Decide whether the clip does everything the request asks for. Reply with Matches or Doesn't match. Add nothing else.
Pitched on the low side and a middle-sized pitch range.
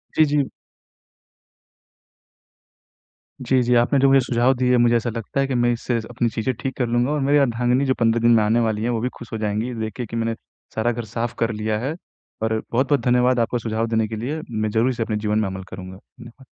Doesn't match